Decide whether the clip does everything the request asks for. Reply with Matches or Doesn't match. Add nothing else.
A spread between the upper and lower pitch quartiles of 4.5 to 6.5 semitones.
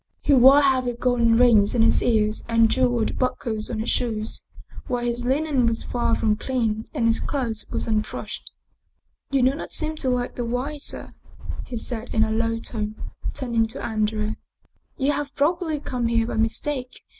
Doesn't match